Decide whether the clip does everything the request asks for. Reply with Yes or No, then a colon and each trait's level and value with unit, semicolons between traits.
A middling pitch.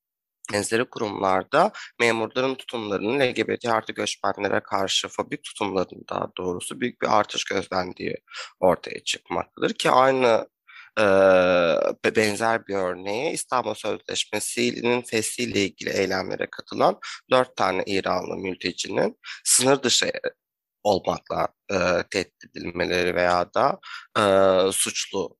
No: low, 110 Hz